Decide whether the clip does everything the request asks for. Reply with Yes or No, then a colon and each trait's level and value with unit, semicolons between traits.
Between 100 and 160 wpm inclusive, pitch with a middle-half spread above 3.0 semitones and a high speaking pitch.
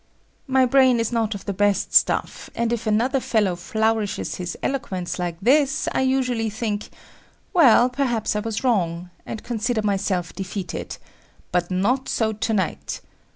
Yes: average, 155 wpm; average, 4.2 semitones; high, 220 Hz